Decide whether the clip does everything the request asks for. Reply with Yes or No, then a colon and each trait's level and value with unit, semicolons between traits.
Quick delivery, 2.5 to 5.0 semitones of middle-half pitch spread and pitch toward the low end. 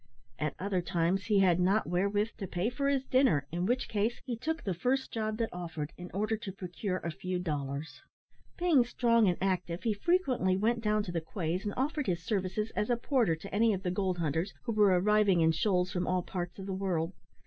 No: fast, 220 wpm; average, 4.1 semitones; high, 195 Hz